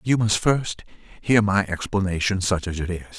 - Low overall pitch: Yes, low, 100 Hz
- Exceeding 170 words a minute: Yes, fast, 205 wpm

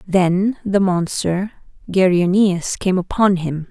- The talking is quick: No, slow, 115 wpm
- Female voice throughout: Yes, female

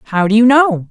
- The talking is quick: Yes, fast, 265 wpm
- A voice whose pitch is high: Yes, high, 225 Hz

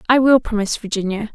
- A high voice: Yes, high, 220 Hz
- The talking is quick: No, average, 180 wpm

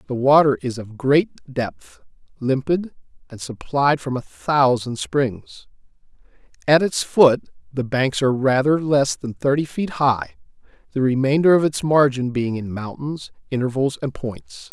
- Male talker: Yes, male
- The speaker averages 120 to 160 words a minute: Yes, average, 145 wpm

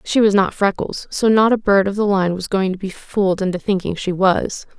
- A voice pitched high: Yes, high, 195 Hz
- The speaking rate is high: Yes, fast, 250 wpm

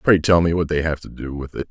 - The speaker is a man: Yes, male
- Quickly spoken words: Yes, fast, 355 wpm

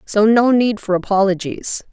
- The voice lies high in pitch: Yes, high, 205 Hz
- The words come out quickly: No, average, 155 wpm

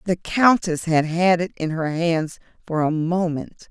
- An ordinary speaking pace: Yes, average, 180 wpm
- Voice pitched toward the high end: No, medium, 170 Hz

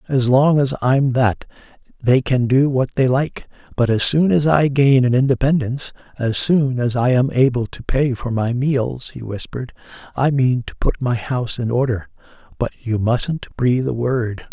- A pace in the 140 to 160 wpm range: No, average, 190 wpm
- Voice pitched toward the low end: Yes, low, 130 Hz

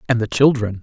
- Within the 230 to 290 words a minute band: No, fast, 220 wpm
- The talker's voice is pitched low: Yes, low, 115 Hz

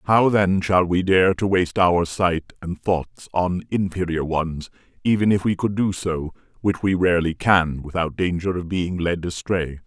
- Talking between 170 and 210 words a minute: Yes, average, 180 wpm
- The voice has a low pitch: Yes, very low, 90 Hz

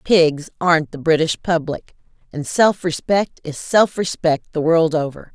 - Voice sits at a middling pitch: Yes, medium, 165 Hz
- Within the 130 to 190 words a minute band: Yes, average, 155 wpm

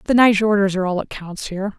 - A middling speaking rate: No, fast, 235 wpm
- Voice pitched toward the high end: Yes, high, 200 Hz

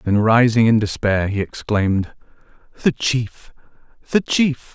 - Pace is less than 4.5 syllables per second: Yes, 4.2 syllables/s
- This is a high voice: No, low, 115 Hz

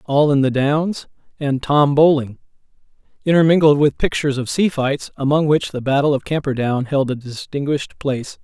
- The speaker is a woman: No, male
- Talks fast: No, average, 165 wpm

